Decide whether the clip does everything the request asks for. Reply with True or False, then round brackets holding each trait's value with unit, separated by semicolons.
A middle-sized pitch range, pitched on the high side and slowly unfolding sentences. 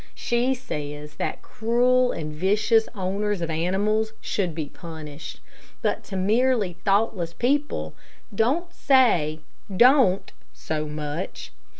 False (7.0 semitones; 200 Hz; 110 wpm)